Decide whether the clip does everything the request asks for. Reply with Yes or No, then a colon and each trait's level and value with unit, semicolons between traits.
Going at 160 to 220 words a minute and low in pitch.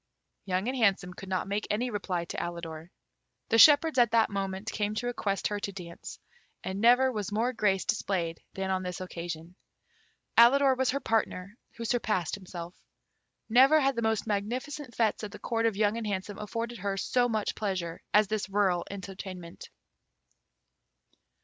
No: average, 170 wpm; high, 205 Hz